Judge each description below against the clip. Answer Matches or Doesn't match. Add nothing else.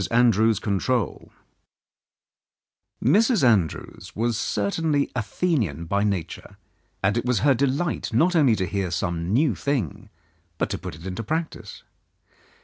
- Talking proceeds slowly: Matches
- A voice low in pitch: Matches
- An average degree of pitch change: Doesn't match